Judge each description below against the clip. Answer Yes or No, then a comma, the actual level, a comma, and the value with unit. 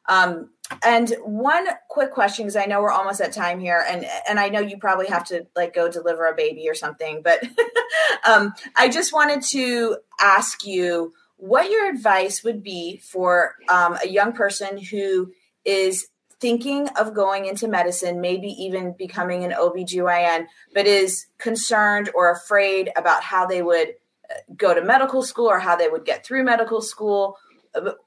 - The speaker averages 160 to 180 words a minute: Yes, average, 170 wpm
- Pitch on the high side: Yes, high, 200 Hz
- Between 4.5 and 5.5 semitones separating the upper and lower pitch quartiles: Yes, average, 4.8 semitones